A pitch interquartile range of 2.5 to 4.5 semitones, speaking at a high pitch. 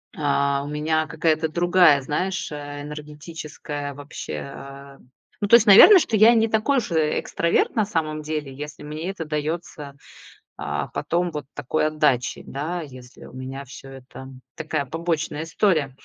No: average, 3.0 semitones; medium, 150 Hz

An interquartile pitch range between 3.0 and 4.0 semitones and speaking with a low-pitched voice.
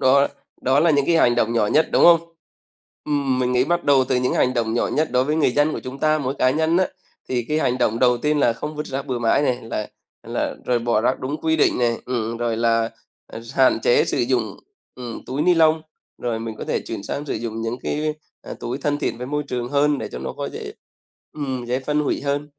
Yes: average, 3.7 semitones; low, 130 Hz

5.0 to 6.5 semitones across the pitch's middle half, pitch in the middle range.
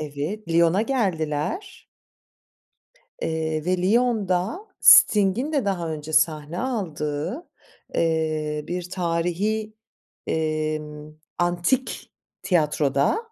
Yes: wide, 5.4 semitones; medium, 170 Hz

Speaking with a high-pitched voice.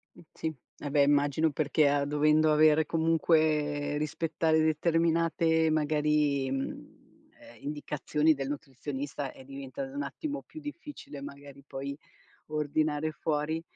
No: medium, 150 Hz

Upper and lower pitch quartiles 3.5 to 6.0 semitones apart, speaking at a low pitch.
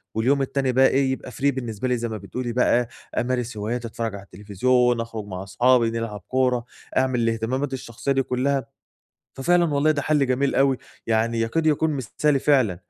No: average, 2.9 semitones; low, 125 Hz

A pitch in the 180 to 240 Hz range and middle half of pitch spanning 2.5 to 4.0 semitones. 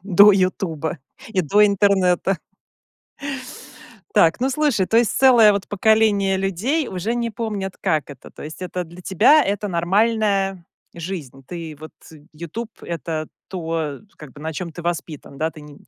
No: medium, 185 Hz; average, 4.4 semitones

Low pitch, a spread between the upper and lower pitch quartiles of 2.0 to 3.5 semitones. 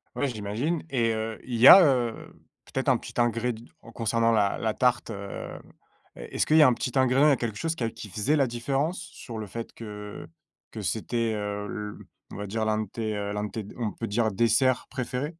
Yes: low, 115 Hz; average, 3.2 semitones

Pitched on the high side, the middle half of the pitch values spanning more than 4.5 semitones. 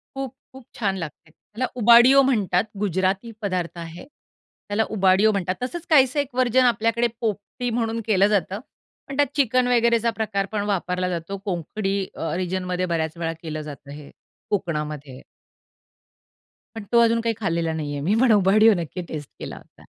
Yes: high, 200 Hz; average, 5.1 semitones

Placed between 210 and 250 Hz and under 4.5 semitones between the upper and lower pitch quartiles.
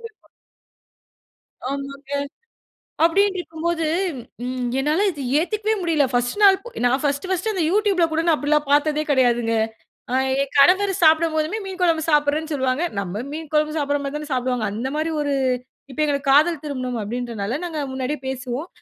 No: very high, 295 Hz; average, 4.0 semitones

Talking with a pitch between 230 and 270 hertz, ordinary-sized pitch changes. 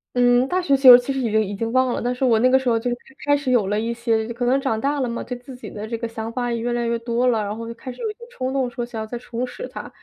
No: high, 245 Hz; narrow, 2.0 semitones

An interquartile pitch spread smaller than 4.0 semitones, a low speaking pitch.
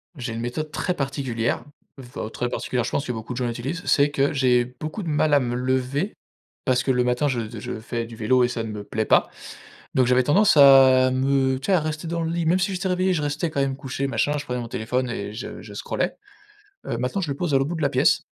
Yes: average, 3.5 semitones; low, 130 Hz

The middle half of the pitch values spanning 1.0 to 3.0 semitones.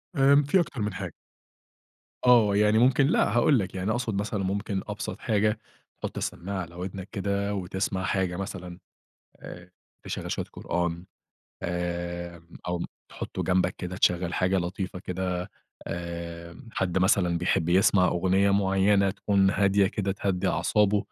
Yes: narrow, 2.4 semitones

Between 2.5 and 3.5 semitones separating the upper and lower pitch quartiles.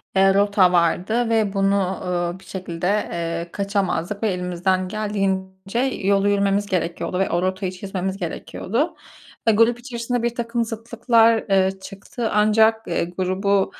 Yes: average, 3.0 semitones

